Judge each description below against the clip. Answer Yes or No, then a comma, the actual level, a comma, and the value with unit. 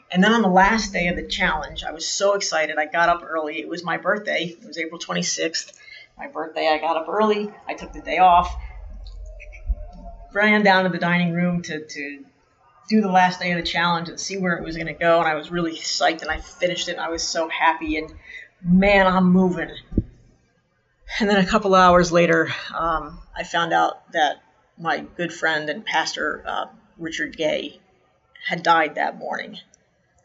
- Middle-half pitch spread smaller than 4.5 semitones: Yes, average, 2.8 semitones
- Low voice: No, medium, 170 Hz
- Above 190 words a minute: Yes, average, 200 wpm